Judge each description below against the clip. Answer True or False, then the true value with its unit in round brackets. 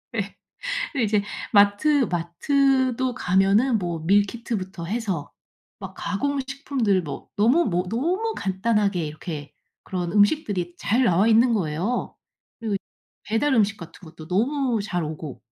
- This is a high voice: True (205 Hz)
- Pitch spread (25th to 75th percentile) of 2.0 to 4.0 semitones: False (5.6 semitones)